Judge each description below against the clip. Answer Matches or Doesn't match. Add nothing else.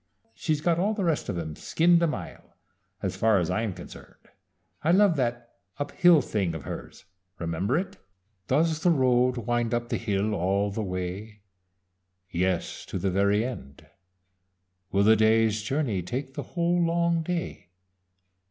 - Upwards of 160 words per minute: Doesn't match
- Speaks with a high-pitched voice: Doesn't match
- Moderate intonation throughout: Doesn't match